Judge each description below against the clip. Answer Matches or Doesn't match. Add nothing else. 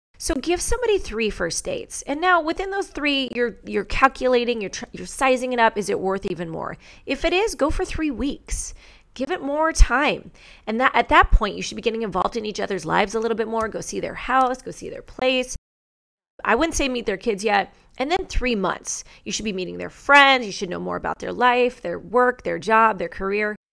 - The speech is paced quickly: Matches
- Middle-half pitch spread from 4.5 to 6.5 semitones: Matches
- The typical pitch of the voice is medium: Doesn't match